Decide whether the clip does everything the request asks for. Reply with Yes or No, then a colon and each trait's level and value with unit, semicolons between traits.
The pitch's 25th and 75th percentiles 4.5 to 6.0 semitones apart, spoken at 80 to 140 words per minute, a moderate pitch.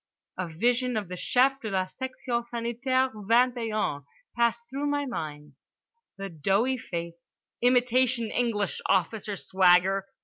No: average, 4.8 semitones; slow, 135 wpm; high, 230 Hz